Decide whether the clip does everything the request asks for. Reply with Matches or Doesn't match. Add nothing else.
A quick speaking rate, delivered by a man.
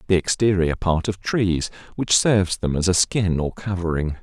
Doesn't match